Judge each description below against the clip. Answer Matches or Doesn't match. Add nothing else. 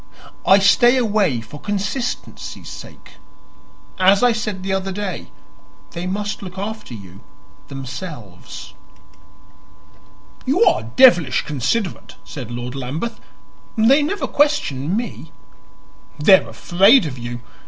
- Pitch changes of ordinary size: Doesn't match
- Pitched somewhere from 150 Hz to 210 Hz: Matches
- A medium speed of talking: Doesn't match